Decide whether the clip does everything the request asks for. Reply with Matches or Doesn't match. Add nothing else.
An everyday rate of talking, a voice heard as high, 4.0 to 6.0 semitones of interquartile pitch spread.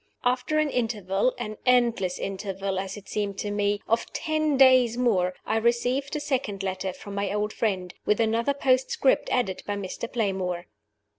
Matches